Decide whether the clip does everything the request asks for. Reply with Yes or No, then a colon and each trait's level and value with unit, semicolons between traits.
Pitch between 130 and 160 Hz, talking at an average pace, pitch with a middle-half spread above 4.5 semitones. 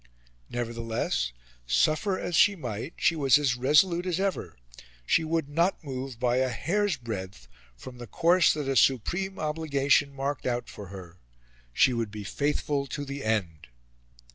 Yes: low, 135 Hz; average, 155 wpm; wide, 5.5 semitones